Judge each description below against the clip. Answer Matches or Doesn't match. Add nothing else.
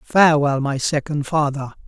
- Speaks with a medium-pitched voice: Matches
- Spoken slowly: Matches